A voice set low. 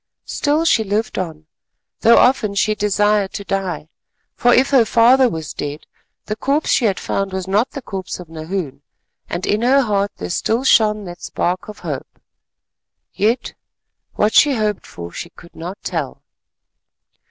No: high, 205 Hz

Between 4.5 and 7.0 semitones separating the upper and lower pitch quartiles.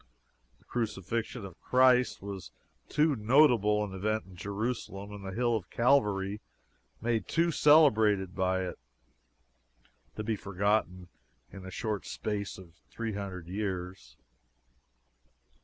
No: average, 3.4 semitones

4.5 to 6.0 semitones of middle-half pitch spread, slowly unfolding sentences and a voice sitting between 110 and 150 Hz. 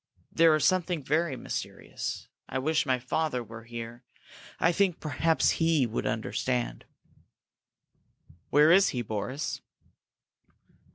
Yes: average, 5.3 semitones; slow, 115 wpm; medium, 140 Hz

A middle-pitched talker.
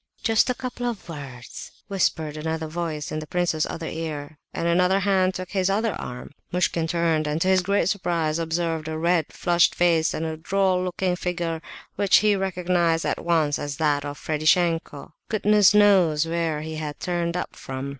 Yes: medium, 170 Hz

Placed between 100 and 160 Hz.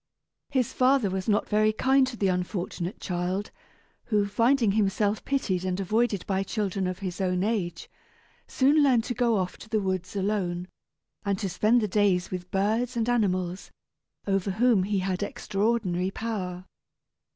No: high, 200 Hz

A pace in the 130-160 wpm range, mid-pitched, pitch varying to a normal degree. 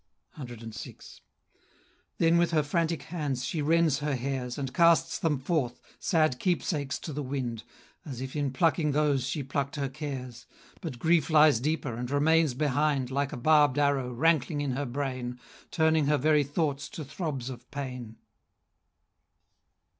Yes: average, 155 wpm; medium, 145 Hz; average, 3.2 semitones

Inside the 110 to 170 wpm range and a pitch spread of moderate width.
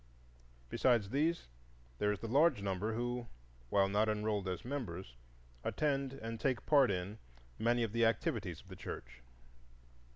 Yes: average, 150 wpm; average, 4.3 semitones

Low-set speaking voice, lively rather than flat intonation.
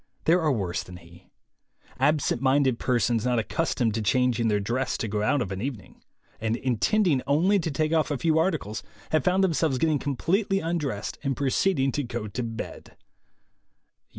Yes: low, 130 Hz; wide, 5.8 semitones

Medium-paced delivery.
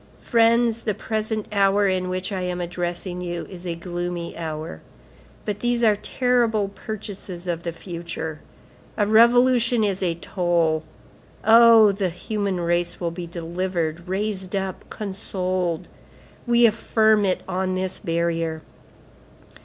No: slow, 130 wpm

